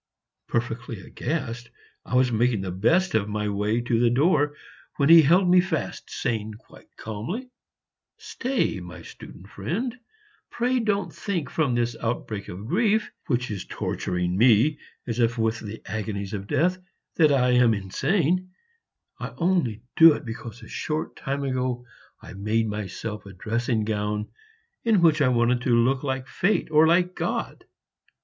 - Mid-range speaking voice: No, low, 120 Hz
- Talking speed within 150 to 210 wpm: Yes, average, 155 wpm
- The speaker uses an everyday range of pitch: No, wide, 6.7 semitones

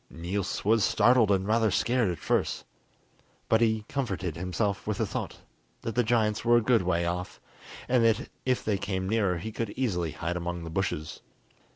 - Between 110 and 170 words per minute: No, average, 185 wpm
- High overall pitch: No, low, 105 Hz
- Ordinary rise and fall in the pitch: Yes, average, 4.2 semitones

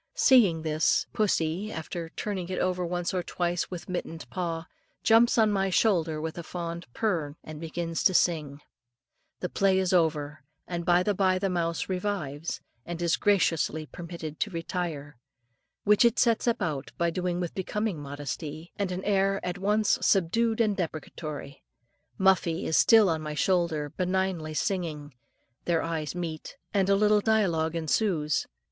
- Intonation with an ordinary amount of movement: Yes, average, 3.4 semitones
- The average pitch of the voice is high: No, medium, 175 Hz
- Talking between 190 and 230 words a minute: No, average, 155 wpm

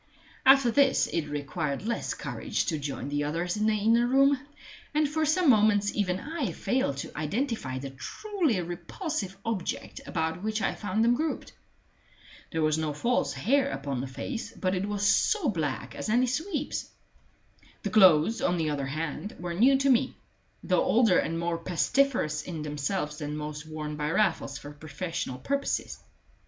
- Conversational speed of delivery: Yes, average, 170 wpm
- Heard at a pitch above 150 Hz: Yes, medium, 185 Hz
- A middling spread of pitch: No, wide, 8.3 semitones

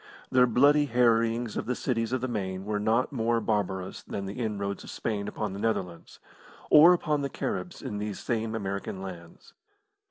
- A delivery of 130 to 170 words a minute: No, average, 180 wpm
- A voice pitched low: Yes, low, 110 Hz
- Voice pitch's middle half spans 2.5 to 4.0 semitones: Yes, average, 3.7 semitones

